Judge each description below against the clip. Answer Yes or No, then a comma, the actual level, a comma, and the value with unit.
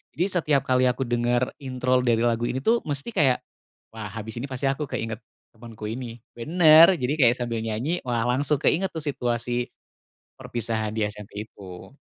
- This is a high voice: No, low, 125 Hz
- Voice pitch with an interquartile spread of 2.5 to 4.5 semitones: Yes, average, 3.4 semitones